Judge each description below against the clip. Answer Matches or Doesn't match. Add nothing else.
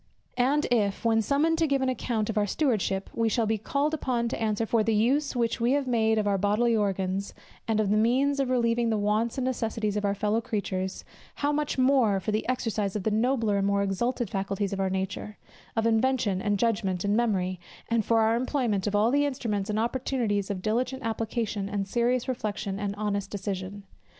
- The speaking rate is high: Matches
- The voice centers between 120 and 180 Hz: Doesn't match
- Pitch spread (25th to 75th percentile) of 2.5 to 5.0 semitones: Matches